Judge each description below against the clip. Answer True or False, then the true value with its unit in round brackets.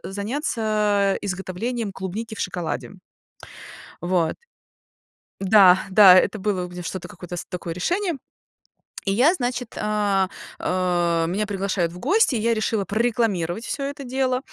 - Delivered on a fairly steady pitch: False (4.2 semitones)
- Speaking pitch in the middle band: False (200 Hz)